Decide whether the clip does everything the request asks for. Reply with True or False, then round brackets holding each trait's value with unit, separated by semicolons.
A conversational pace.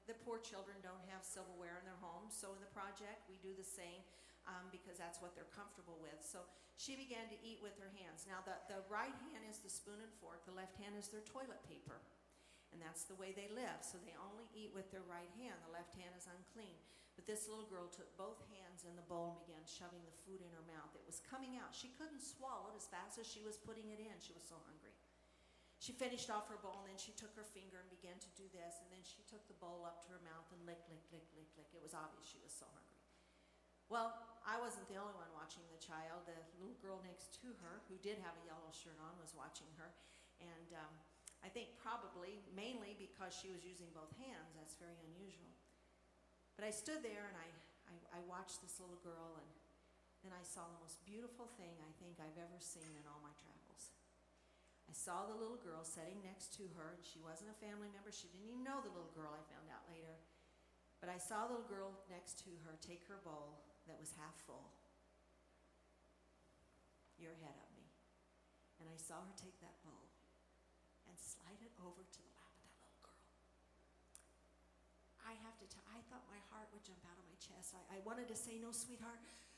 False (225 wpm)